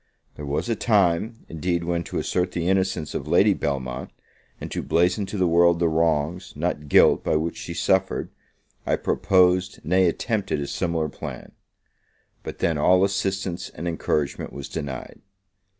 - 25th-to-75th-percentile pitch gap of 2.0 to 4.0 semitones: Yes, average, 3.1 semitones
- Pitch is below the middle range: Yes, very low, 85 Hz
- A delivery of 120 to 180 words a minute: Yes, average, 160 wpm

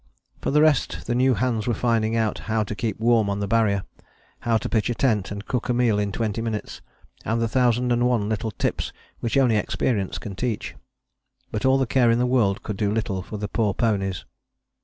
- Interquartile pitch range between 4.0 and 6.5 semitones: No, average, 2.7 semitones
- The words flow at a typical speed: No, fast, 220 wpm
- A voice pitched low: Yes, low, 115 Hz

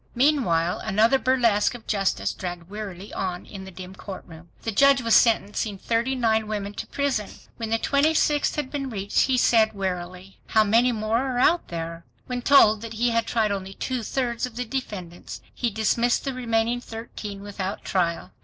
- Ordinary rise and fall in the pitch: Yes, average, 4.0 semitones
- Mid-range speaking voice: No, high, 220 Hz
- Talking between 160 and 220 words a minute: Yes, average, 180 wpm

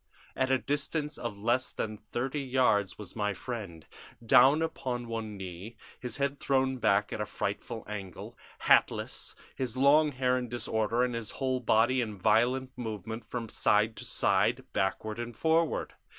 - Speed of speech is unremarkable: Yes, average, 160 wpm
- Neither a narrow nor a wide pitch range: Yes, average, 3.6 semitones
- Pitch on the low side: Yes, low, 120 Hz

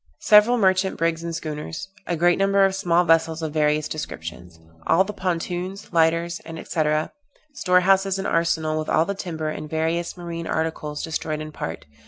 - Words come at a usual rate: Yes, average, 170 wpm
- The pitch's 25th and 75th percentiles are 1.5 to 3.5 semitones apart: Yes, average, 2.9 semitones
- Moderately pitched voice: Yes, medium, 165 Hz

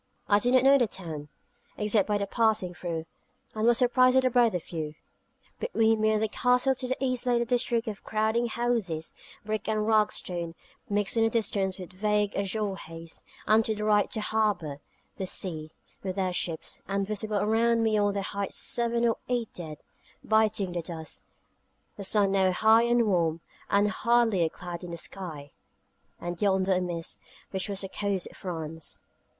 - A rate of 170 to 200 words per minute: Yes, average, 185 wpm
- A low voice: No, high, 205 Hz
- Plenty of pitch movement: No, average, 3.8 semitones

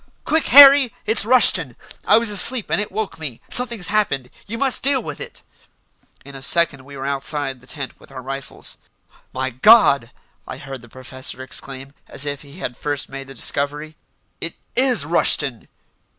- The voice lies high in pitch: No, medium, 145 Hz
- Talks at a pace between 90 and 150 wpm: No, average, 175 wpm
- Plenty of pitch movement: Yes, wide, 8.2 semitones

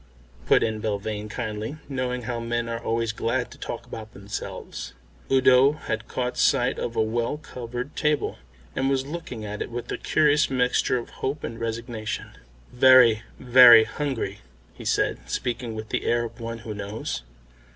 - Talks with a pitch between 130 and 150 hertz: No, low, 120 Hz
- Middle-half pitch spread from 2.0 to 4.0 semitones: Yes, narrow, 2.5 semitones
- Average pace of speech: Yes, average, 165 wpm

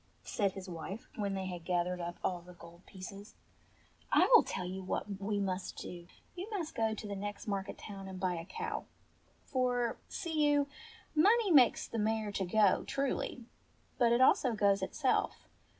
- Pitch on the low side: No, high, 200 Hz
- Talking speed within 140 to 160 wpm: No, average, 180 wpm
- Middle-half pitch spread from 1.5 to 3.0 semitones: No, average, 4.8 semitones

